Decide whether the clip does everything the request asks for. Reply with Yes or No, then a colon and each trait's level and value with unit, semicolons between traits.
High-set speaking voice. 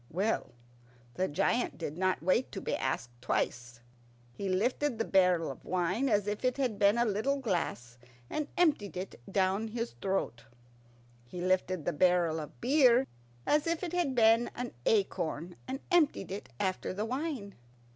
Yes: high, 200 Hz